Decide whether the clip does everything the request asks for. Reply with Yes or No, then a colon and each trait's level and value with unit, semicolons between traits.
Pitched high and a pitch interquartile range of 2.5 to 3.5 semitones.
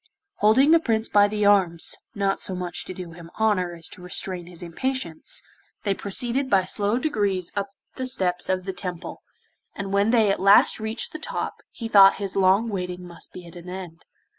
Yes: high, 195 Hz; average, 3.2 semitones